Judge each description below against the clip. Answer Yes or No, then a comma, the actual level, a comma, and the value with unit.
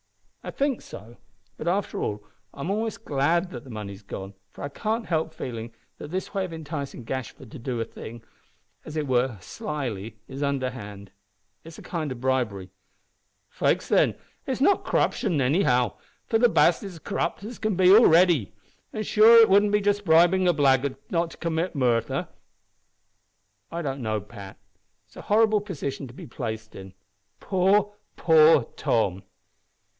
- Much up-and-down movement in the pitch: Yes, wide, 7.9 semitones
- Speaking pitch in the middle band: Yes, medium, 145 Hz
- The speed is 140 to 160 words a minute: No, average, 170 wpm